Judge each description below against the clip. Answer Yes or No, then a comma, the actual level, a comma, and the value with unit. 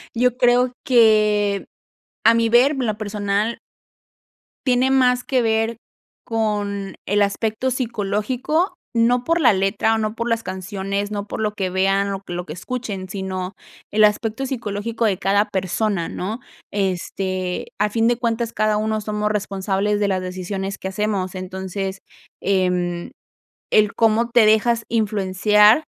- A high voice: Yes, high, 210 Hz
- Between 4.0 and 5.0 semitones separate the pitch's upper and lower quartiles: No, average, 2.9 semitones